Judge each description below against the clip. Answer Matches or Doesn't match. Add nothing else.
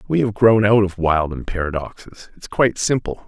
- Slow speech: Doesn't match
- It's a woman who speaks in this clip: Doesn't match